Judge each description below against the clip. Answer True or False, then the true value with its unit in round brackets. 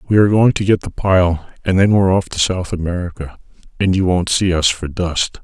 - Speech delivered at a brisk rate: True (230 wpm)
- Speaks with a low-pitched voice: True (90 Hz)